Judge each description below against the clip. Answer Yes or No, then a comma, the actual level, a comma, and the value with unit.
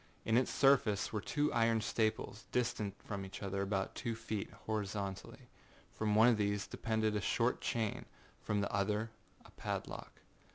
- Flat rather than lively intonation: Yes, narrow, 2.1 semitones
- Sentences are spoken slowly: No, average, 160 wpm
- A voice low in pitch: Yes, low, 110 Hz